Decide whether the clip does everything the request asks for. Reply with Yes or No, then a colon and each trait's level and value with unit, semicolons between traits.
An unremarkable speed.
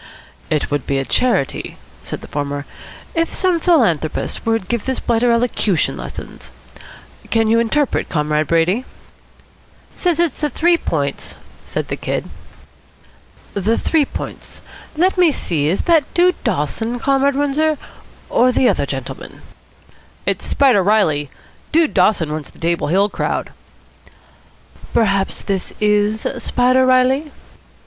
No: slow, 130 wpm